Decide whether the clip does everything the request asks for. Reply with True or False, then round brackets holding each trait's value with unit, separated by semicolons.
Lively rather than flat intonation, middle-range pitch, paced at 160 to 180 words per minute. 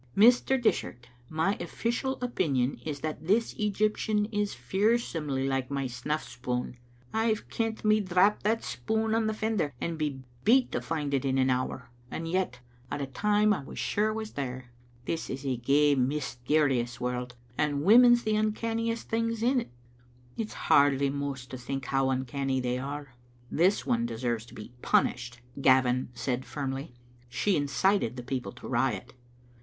True (8.7 semitones; 145 Hz; 165 wpm)